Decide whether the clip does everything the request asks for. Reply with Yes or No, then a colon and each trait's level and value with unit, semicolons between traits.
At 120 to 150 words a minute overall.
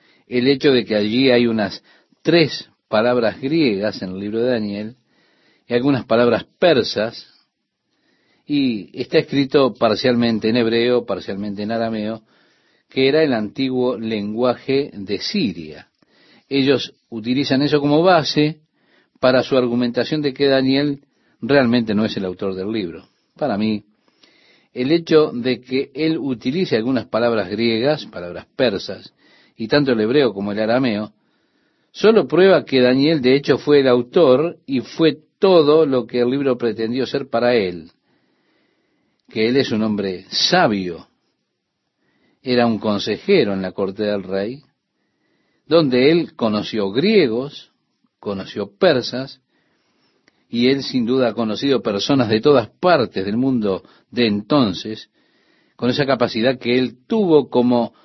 Yes: average, 140 wpm